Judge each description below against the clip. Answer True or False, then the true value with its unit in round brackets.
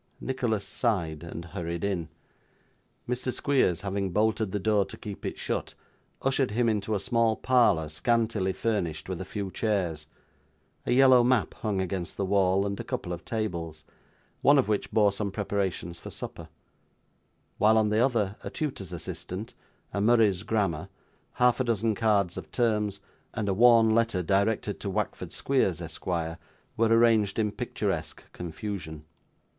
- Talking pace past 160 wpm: False (155 wpm)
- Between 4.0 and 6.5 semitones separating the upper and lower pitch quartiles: False (3.6 semitones)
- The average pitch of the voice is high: False (105 Hz)